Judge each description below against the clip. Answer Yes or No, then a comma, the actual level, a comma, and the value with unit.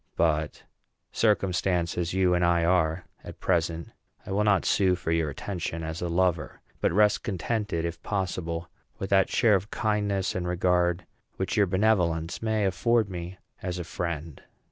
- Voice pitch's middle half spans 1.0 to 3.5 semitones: Yes, average, 2.7 semitones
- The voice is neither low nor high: No, very low, 90 Hz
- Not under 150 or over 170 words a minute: Yes, average, 165 wpm